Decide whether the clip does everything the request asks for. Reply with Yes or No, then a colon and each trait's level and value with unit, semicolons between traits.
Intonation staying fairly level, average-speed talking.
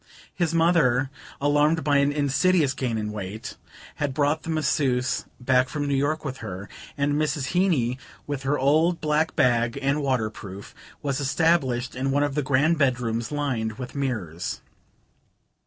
No: average, 3.3 semitones; average, 155 wpm